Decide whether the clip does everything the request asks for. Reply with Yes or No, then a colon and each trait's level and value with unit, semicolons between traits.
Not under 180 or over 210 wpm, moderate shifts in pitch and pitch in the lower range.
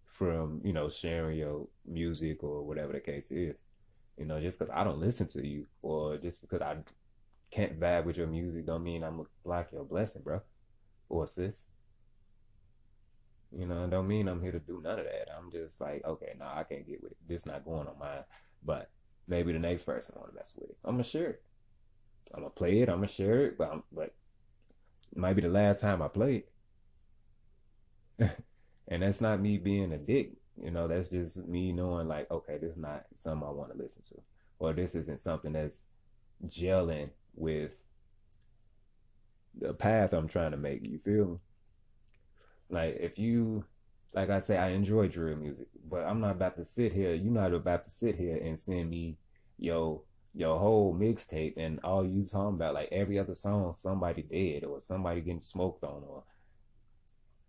Yes: average, 200 wpm; average, 3.8 semitones; very low, 90 Hz